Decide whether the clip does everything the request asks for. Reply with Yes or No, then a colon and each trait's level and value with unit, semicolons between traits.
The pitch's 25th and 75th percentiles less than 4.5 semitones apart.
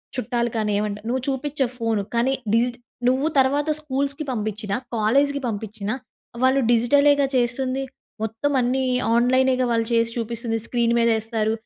Yes: average, 2.9 semitones